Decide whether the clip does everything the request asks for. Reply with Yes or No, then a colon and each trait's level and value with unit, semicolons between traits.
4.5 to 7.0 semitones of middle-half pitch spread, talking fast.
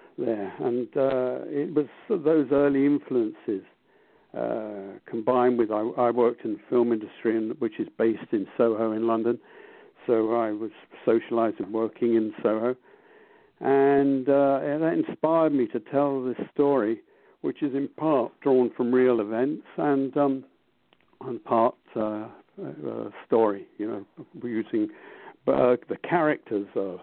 No: average, 5.2 semitones; average, 145 wpm